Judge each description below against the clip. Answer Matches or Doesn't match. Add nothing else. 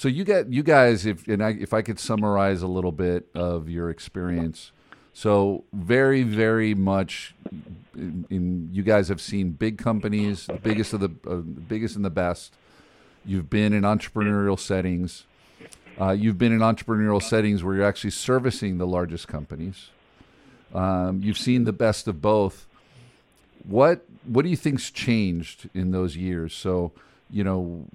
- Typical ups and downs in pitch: Matches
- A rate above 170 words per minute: Doesn't match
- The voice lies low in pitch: Matches